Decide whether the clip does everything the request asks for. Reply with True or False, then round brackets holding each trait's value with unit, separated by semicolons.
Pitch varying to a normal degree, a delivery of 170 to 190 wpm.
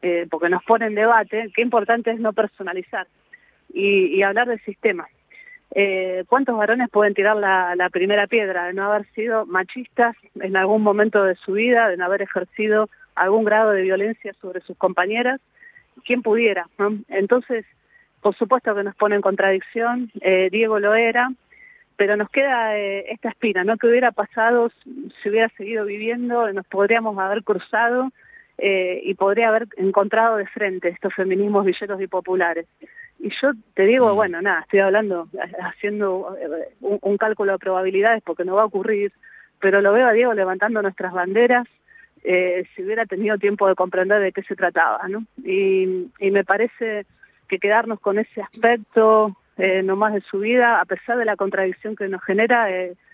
True (3.2 semitones; 175 wpm)